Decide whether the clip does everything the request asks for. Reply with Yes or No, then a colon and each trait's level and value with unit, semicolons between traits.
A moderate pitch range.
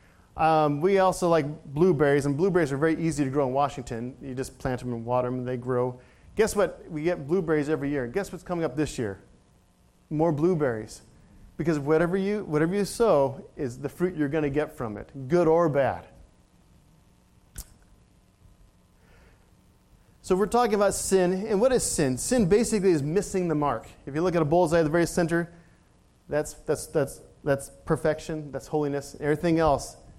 Yes: average, 4.5 semitones